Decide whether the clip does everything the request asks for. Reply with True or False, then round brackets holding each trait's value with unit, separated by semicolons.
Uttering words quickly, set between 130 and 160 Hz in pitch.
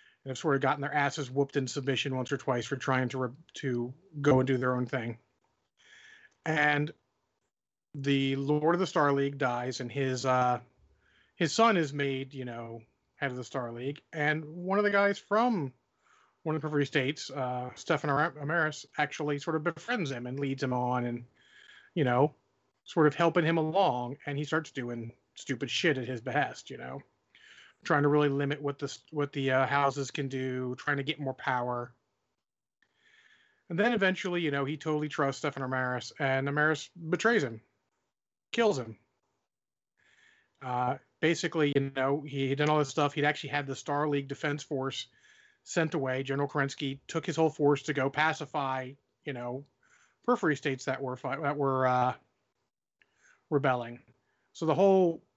False (175 wpm; 140 Hz)